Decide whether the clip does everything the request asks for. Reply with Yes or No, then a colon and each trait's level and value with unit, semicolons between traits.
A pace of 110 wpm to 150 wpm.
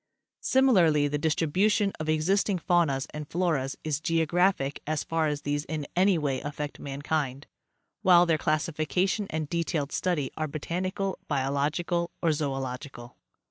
Yes: slow, 135 wpm